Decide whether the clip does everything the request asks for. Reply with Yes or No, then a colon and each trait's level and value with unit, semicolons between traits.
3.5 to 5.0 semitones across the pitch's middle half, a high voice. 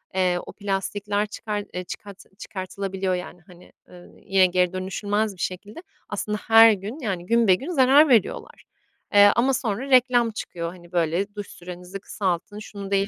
No: average, 2.9 semitones; high, 200 Hz